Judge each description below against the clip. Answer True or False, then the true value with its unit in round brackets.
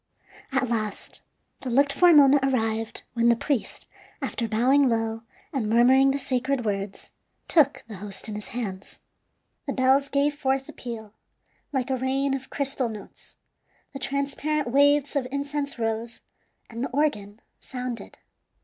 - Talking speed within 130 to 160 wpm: True (150 wpm)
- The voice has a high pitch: True (260 Hz)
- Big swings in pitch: False (3.7 semitones)